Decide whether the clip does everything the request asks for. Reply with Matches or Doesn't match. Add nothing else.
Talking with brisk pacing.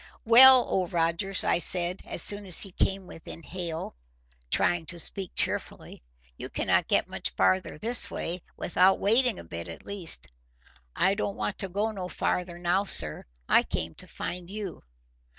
Doesn't match